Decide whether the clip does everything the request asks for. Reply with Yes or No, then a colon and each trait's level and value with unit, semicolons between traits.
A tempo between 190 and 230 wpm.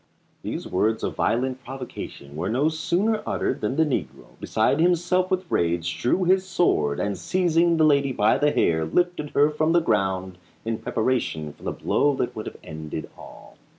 No: average, 180 wpm